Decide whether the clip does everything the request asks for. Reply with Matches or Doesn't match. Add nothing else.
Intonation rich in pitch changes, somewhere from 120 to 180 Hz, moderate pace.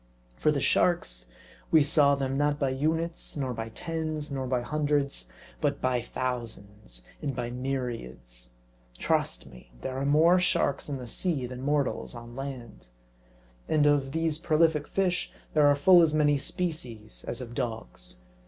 Doesn't match